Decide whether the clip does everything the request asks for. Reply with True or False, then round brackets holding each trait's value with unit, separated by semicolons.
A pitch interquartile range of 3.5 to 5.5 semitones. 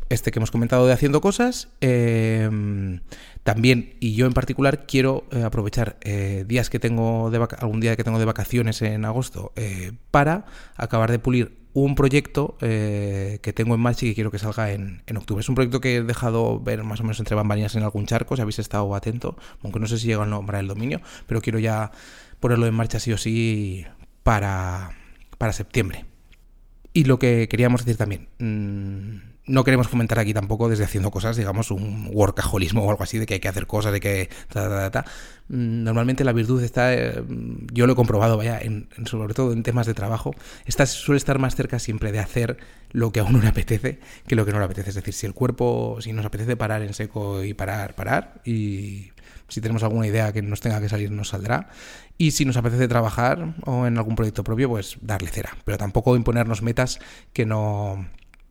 False (2.7 semitones)